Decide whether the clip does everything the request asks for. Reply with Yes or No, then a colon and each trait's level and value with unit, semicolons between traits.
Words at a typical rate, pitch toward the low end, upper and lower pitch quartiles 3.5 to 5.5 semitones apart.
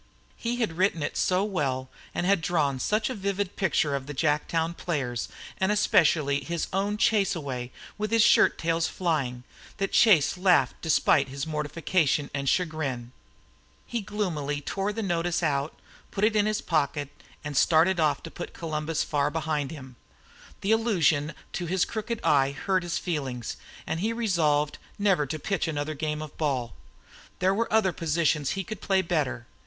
No: average, 170 wpm; medium, 165 Hz; average, 4.9 semitones